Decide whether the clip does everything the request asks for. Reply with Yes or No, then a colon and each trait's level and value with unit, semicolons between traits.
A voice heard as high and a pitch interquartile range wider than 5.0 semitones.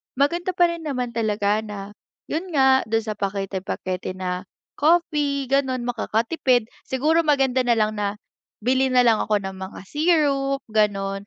Yes: high, 245 Hz; wide, 5.4 semitones